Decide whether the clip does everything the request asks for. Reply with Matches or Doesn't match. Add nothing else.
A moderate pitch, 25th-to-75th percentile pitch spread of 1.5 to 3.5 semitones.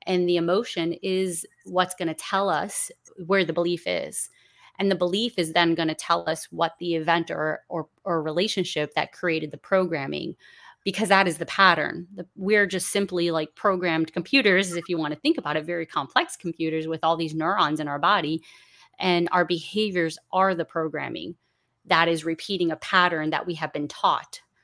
Matches